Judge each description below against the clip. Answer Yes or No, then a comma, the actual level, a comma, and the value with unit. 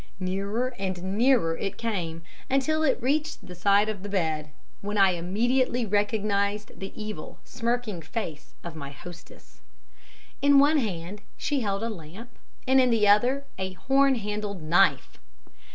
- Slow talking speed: No, average, 150 wpm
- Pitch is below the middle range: No, high, 205 Hz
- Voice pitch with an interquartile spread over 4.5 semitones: Yes, average, 5.0 semitones